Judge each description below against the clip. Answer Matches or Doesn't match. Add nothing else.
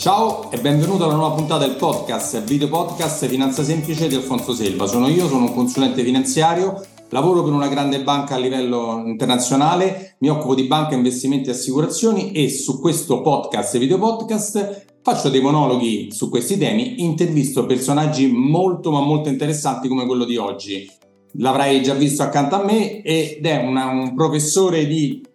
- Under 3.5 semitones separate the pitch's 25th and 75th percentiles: Doesn't match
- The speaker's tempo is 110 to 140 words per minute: Doesn't match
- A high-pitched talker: Doesn't match